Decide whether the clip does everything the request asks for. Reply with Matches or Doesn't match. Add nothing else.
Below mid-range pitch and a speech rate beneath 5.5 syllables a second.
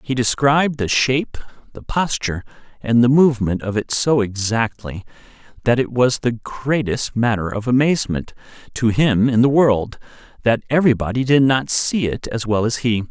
Matches